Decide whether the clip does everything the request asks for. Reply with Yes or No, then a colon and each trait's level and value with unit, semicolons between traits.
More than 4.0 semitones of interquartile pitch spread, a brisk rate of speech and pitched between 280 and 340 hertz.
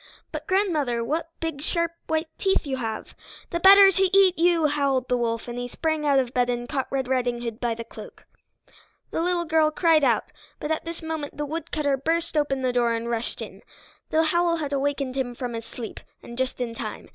Yes: average, 4.9 semitones; fast, 215 wpm; very high, 285 Hz